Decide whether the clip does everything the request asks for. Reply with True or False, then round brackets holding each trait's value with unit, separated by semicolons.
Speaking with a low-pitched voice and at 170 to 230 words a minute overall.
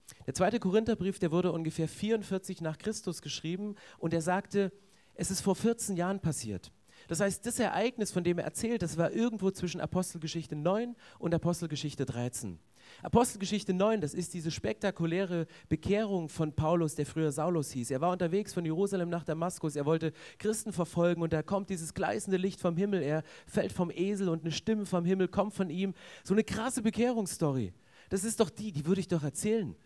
False (180 Hz; 185 wpm)